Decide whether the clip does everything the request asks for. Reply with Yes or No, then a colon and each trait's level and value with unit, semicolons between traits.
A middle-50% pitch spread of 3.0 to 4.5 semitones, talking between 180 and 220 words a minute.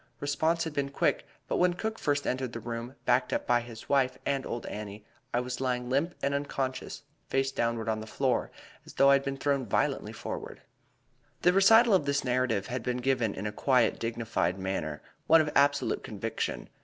Yes: average, 3.4 semitones; average, 195 wpm